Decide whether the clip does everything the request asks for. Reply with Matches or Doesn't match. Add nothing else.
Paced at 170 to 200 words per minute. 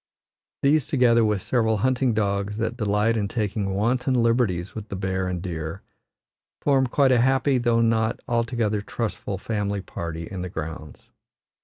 Doesn't match